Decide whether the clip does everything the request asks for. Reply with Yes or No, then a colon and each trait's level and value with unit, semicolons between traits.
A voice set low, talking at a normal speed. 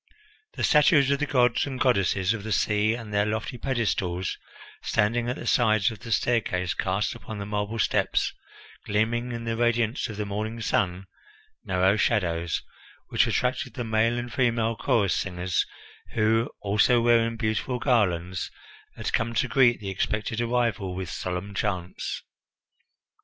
Yes: low, 110 Hz; average, 150 wpm